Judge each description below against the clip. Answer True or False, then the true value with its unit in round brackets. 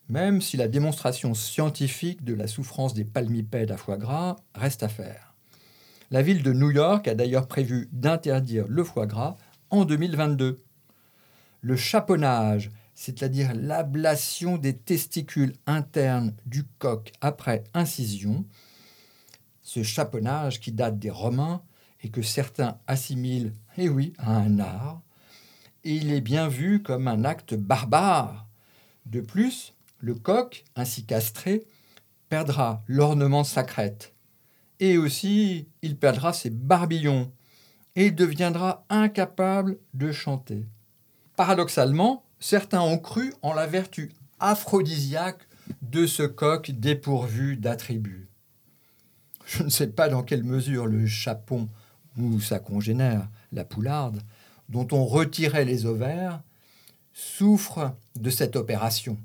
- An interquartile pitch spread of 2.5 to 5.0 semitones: False (5.5 semitones)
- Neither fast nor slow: False (125 wpm)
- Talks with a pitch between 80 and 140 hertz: True (135 Hz)